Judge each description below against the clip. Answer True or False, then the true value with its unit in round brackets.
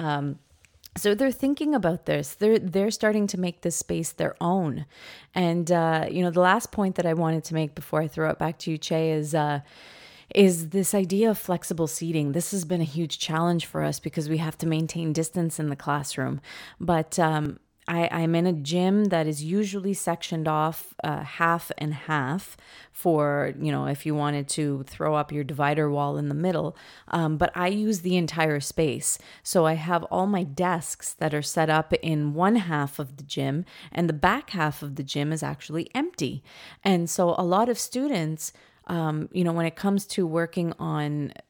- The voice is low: False (165 Hz)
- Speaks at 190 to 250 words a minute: True (200 wpm)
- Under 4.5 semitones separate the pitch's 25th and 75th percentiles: True (2.9 semitones)